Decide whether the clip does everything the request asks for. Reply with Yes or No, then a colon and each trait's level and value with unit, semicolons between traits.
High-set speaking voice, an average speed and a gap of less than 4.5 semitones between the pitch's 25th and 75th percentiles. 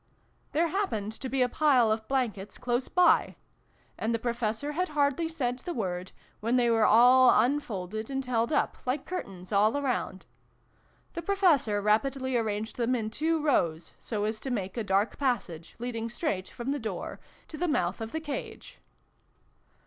No: high, 240 Hz; average, 170 wpm; average, 4.8 semitones